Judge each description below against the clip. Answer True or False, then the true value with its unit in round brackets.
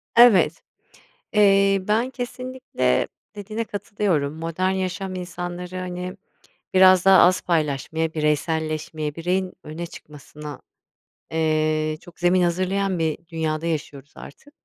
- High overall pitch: False (175 Hz)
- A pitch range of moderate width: True (3.6 semitones)